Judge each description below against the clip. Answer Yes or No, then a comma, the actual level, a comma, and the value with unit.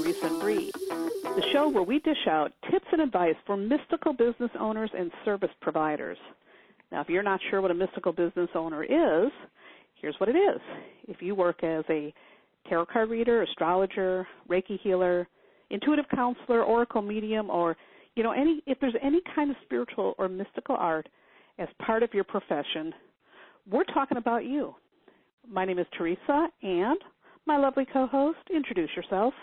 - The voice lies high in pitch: Yes, high, 220 Hz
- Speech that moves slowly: No, average, 165 wpm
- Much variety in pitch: Yes, wide, 8.1 semitones